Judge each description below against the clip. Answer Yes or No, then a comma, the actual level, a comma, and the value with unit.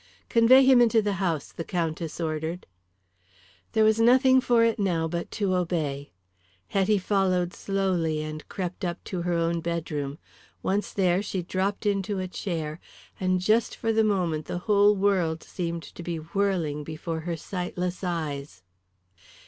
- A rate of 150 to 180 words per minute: Yes, average, 155 wpm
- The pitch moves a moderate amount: Yes, average, 3.6 semitones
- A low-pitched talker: No, medium, 180 Hz